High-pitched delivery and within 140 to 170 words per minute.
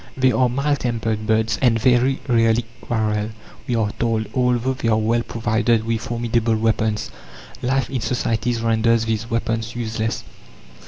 No: low, 115 Hz; average, 150 wpm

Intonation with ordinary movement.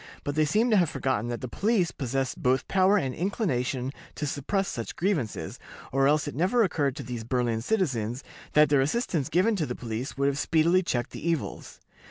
No: wide, 6.3 semitones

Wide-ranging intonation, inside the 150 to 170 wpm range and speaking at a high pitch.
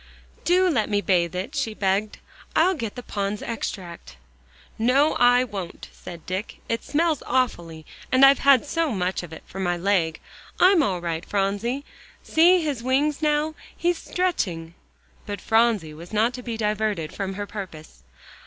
Yes: wide, 6.9 semitones; average, 160 wpm; high, 215 Hz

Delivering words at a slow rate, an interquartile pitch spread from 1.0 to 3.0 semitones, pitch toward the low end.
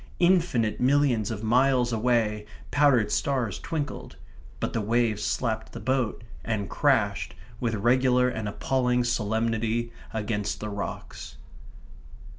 Yes: slow, 115 wpm; average, 2.7 semitones; low, 115 Hz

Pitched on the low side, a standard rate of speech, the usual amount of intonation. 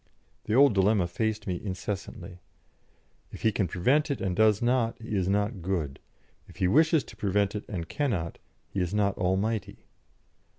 Yes: low, 100 Hz; average, 170 wpm; average, 3.2 semitones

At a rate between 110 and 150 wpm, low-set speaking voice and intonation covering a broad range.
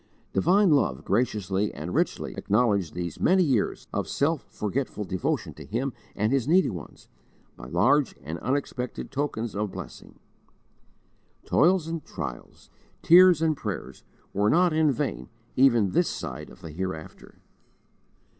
Yes: slow, 135 wpm; low, 120 Hz; wide, 7.9 semitones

